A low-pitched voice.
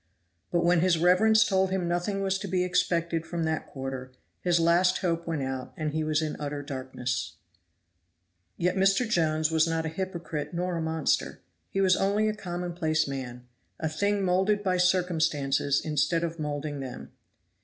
No: medium, 170 Hz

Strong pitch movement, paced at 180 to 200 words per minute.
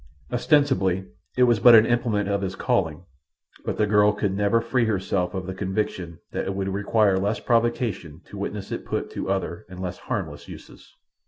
No: average, 3.1 semitones; average, 185 wpm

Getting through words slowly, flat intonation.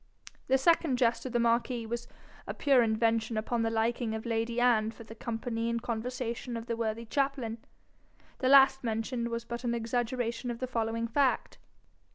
No: average, 180 wpm; narrow, 1.6 semitones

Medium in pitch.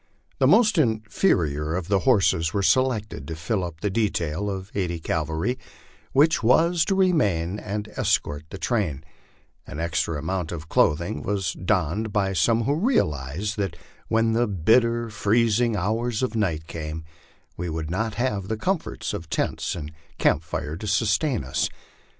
No: low, 100 Hz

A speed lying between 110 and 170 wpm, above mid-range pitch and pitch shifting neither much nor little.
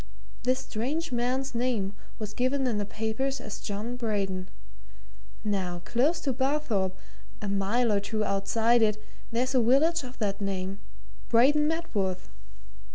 Yes: average, 140 wpm; high, 230 Hz; average, 4.4 semitones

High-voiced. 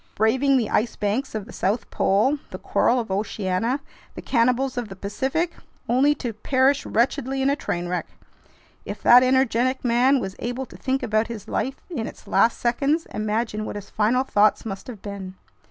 Yes: high, 235 Hz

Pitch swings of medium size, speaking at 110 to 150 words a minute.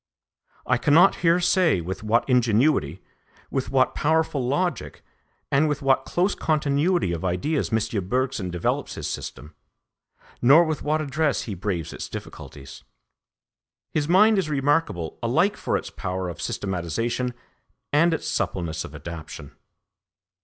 No: wide, 8.9 semitones; slow, 135 wpm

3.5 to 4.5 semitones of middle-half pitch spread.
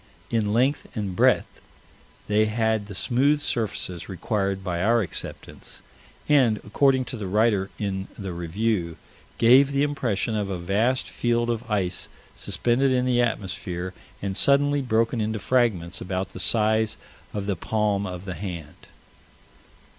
Yes: average, 3.8 semitones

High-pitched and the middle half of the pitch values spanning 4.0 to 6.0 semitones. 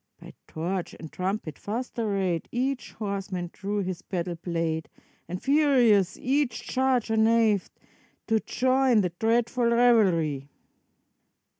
Yes: high, 210 Hz; average, 5.1 semitones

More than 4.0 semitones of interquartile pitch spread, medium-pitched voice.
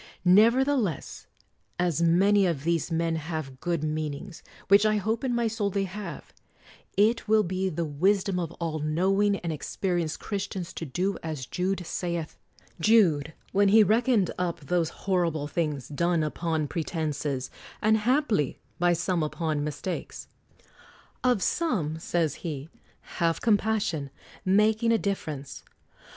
Yes: average, 4.5 semitones; medium, 175 Hz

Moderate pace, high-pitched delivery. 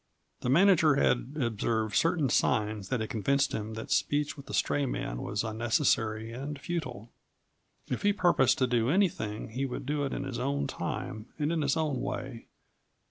No: average, 180 wpm; low, 130 Hz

